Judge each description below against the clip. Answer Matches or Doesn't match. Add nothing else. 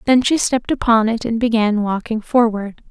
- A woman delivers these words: Matches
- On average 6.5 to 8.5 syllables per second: Doesn't match